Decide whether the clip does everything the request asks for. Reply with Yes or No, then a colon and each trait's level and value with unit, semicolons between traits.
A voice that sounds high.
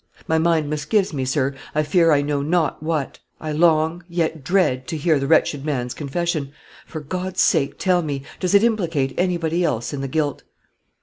No: medium, 155 Hz